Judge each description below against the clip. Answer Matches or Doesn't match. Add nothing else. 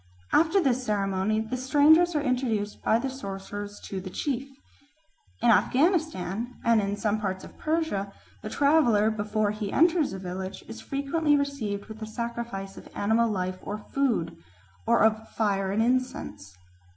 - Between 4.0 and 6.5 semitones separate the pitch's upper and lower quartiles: Matches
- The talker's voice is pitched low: Doesn't match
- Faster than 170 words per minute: Doesn't match